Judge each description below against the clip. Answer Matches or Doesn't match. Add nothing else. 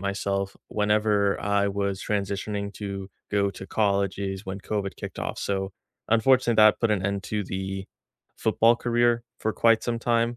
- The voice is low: Matches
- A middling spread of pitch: Doesn't match